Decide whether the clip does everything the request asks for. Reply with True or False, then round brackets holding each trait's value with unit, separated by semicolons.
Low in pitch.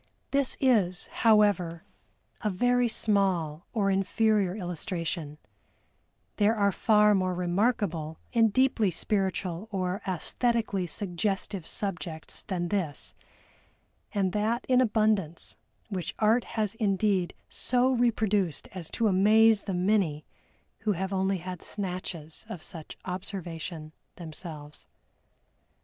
False (195 Hz)